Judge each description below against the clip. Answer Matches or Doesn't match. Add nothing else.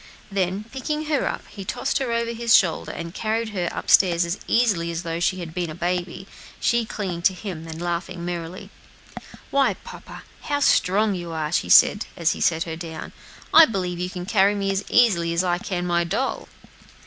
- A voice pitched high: Doesn't match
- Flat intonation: Doesn't match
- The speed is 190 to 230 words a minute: Matches